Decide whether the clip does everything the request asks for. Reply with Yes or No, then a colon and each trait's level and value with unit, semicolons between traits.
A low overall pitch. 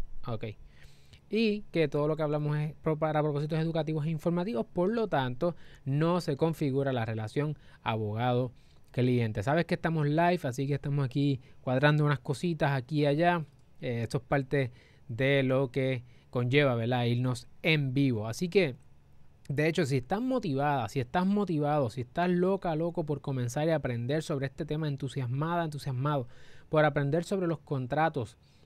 No: medium, 145 Hz